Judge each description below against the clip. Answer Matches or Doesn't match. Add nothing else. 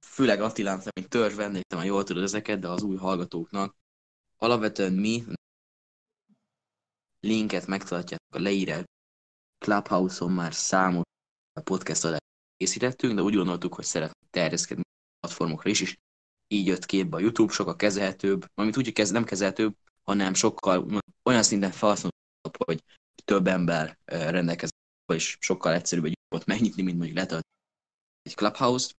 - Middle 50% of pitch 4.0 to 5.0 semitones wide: Doesn't match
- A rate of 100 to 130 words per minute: Doesn't match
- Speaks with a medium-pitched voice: Doesn't match